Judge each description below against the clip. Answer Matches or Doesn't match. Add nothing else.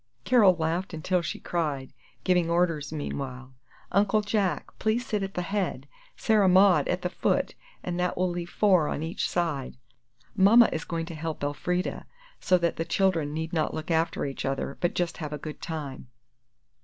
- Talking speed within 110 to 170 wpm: Doesn't match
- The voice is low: Doesn't match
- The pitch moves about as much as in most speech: Matches